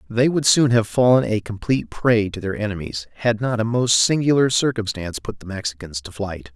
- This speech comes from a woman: No, male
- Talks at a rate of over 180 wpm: Yes, average, 200 wpm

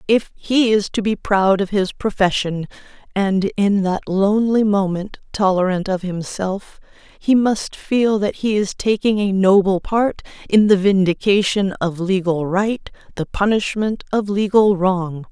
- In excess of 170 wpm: No, average, 150 wpm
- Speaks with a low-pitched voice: No, high, 200 Hz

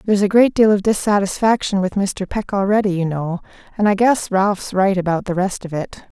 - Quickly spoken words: Yes, fast, 215 wpm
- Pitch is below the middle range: No, high, 195 Hz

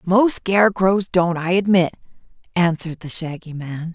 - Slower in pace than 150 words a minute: Yes, slow, 135 wpm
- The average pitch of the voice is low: No, medium, 180 Hz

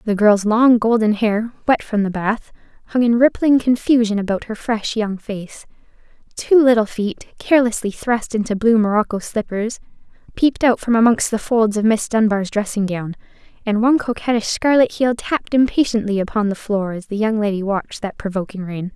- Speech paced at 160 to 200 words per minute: Yes, average, 175 wpm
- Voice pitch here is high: Yes, high, 220 Hz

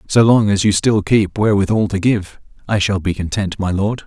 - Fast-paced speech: Yes, fast, 220 wpm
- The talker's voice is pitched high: No, low, 100 Hz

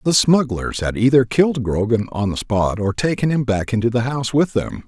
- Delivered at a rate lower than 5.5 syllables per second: Yes, 5.3 syllables/s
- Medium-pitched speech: No, low, 120 Hz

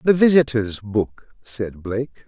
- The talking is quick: No, slow, 130 wpm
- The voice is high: No, low, 120 Hz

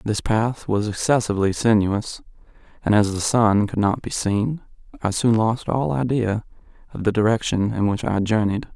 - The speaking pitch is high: No, low, 110 Hz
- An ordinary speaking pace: Yes, average, 170 wpm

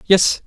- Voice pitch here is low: No, high, 190 Hz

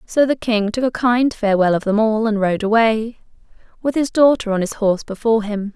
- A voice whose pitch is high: Yes, high, 220 Hz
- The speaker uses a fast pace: Yes, fast, 220 wpm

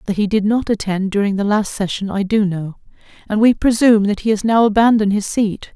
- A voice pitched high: Yes, high, 210 Hz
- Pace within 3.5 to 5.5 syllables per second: No, 5.9 syllables/s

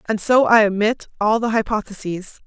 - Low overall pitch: No, high, 220 Hz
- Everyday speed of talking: Yes, average, 170 wpm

